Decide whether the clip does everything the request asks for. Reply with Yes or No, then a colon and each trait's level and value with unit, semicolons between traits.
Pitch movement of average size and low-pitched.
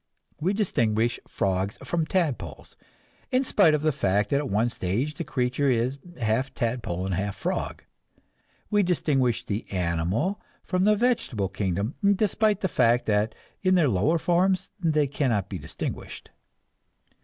No: wide, 8.8 semitones; low, 130 Hz